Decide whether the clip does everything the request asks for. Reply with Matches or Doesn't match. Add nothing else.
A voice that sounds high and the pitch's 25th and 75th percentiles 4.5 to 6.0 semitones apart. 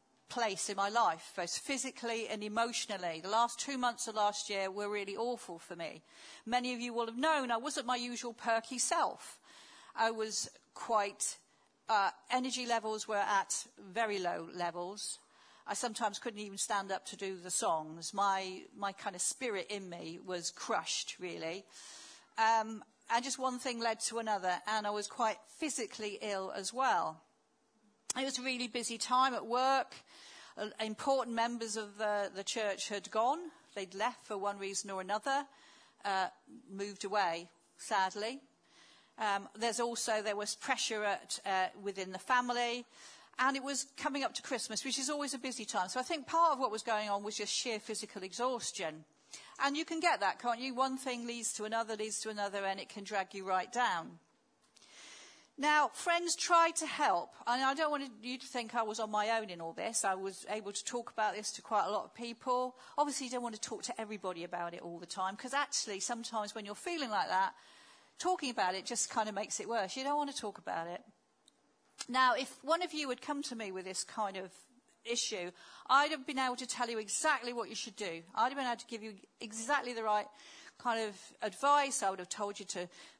Doesn't match